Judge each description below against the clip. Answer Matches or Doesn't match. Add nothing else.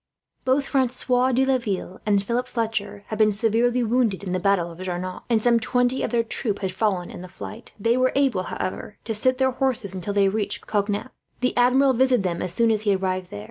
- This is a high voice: Matches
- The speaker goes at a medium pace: Doesn't match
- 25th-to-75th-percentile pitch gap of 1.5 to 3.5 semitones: Doesn't match